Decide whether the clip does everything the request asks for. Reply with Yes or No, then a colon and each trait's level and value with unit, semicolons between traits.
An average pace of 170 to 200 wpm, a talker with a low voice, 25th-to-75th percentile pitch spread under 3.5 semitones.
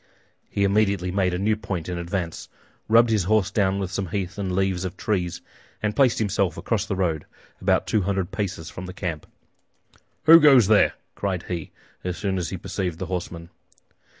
Yes: average, 185 wpm; very low, 95 Hz; narrow, 2.6 semitones